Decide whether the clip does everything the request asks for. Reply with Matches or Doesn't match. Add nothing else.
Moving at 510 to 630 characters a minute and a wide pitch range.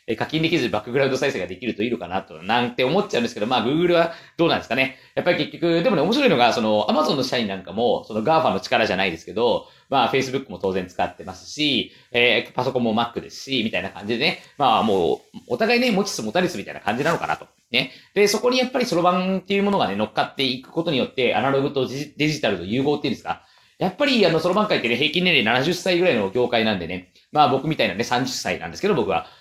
Matches